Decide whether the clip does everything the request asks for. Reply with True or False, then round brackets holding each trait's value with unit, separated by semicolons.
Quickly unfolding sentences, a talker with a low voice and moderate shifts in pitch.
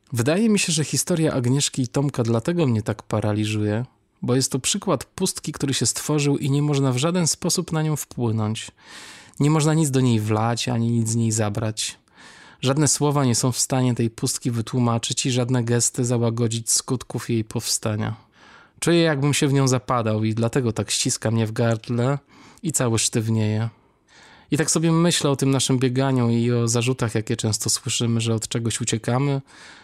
True (180 wpm; 125 Hz; 3.7 semitones)